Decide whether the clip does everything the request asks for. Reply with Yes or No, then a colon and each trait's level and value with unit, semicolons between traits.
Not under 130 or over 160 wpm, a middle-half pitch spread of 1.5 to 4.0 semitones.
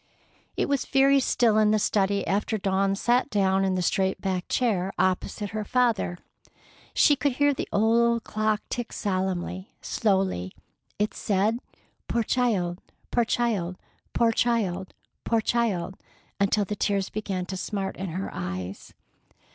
Yes: average, 145 wpm; average, 3.6 semitones